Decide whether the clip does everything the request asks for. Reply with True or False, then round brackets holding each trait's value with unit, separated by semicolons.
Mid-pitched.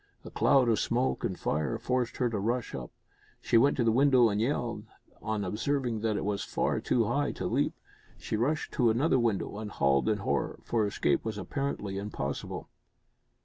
False (115 Hz)